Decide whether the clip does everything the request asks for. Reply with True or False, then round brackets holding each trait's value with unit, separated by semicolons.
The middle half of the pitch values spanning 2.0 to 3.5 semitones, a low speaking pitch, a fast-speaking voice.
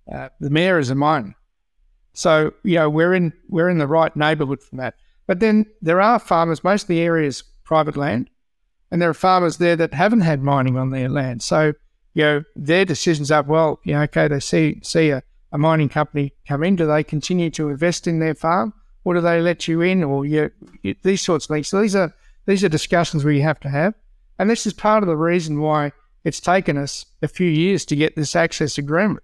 False (2.7 semitones; 160 Hz; 230 wpm)